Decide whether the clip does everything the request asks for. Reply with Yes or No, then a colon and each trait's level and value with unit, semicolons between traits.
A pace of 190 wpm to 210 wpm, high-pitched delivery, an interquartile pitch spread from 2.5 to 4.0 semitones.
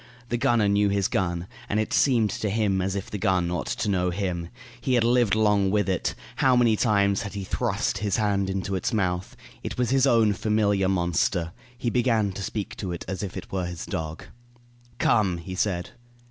No: fast, 205 wpm; low, 100 Hz; average, 2.8 semitones